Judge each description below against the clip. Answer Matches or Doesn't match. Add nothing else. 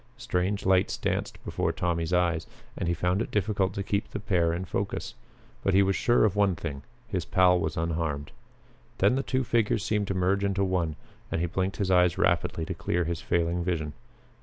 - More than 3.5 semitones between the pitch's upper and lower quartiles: Doesn't match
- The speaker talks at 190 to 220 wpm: Matches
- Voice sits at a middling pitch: Doesn't match